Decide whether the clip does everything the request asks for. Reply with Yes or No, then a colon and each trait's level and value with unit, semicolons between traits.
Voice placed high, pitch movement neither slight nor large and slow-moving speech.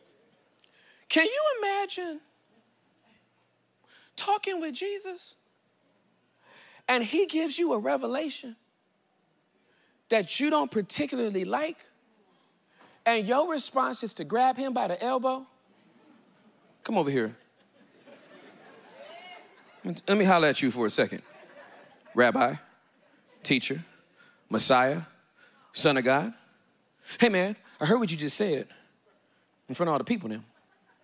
No: very high, 260 Hz; wide, 6.0 semitones; slow, 115 wpm